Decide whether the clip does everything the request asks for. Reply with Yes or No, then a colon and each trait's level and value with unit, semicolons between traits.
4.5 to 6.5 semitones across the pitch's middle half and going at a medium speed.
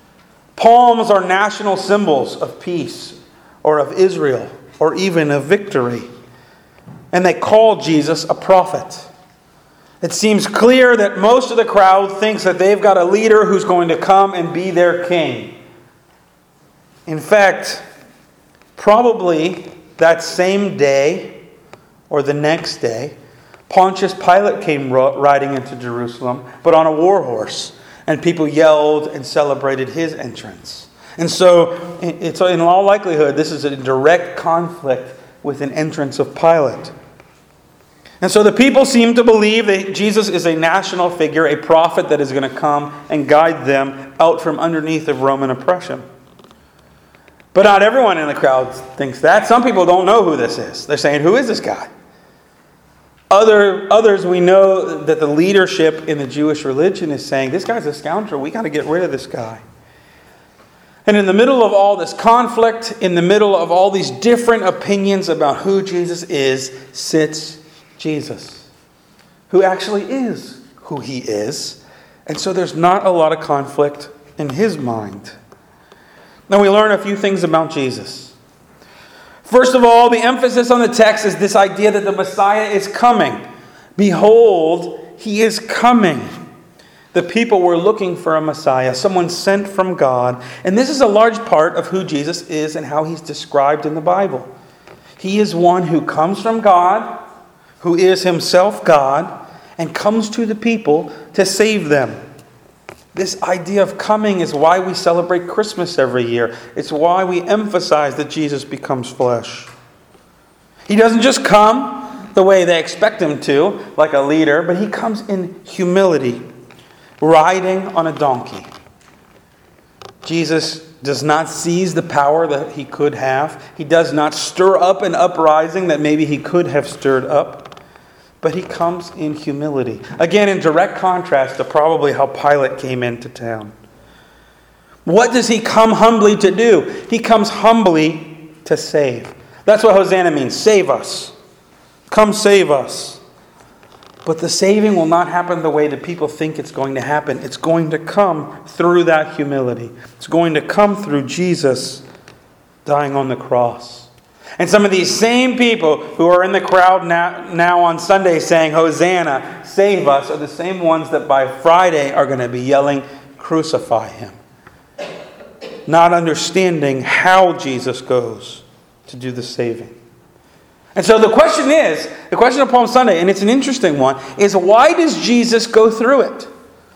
Yes: average, 5.2 semitones; average, 160 wpm